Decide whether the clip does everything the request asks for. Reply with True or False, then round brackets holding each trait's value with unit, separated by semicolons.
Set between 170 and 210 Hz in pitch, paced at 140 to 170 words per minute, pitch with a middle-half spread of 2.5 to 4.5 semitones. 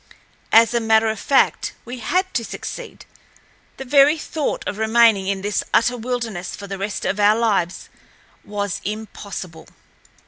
False (220 Hz; 150 wpm; 3.1 semitones)